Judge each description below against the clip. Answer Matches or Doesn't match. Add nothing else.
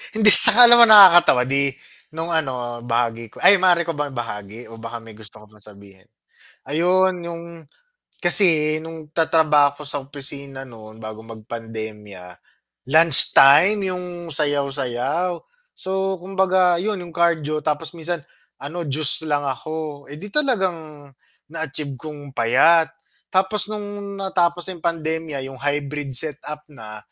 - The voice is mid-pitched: Matches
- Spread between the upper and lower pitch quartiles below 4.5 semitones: Doesn't match